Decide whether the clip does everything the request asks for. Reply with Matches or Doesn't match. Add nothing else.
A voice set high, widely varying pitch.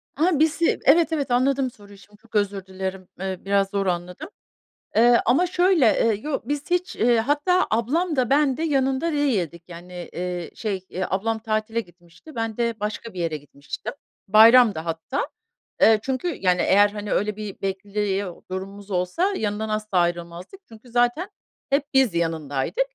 Matches